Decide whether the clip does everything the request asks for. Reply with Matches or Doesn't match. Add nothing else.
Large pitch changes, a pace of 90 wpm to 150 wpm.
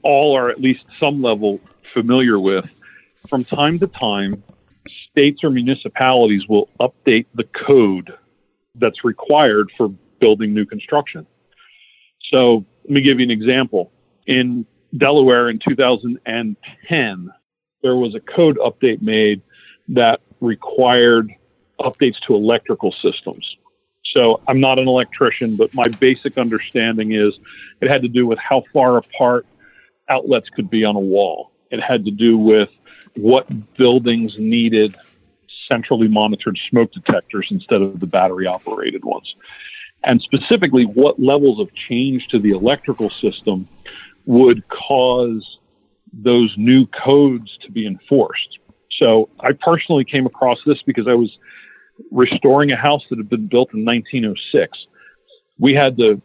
Doesn't match